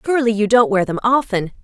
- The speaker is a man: No, female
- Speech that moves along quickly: Yes, fast, 220 wpm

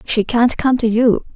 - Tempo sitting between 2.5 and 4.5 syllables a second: Yes, 4.2 syllables/s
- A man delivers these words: No, female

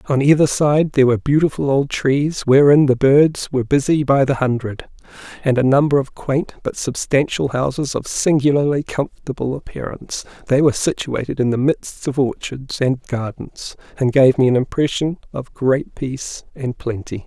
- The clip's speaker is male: Yes, male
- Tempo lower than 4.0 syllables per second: No, 5.0 syllables/s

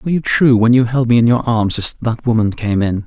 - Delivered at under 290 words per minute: No, fast, 295 wpm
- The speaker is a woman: No, male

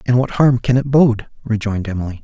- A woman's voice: No, male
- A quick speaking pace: Yes, fast, 215 wpm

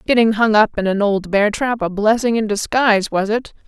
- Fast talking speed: Yes, fast, 230 wpm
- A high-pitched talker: Yes, high, 215 Hz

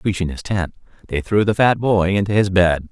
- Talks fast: Yes, fast, 225 wpm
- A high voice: No, very low, 95 Hz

